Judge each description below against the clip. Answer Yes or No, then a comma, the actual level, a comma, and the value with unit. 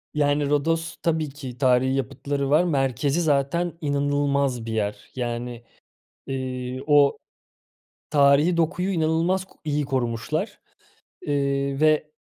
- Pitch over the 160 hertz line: No, medium, 140 Hz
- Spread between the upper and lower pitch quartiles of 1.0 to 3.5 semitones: Yes, average, 2.9 semitones